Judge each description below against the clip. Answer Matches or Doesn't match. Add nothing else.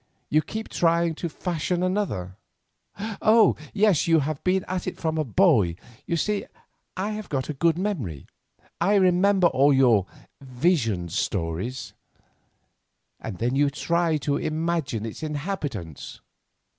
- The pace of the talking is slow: Matches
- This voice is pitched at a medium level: Matches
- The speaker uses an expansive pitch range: Matches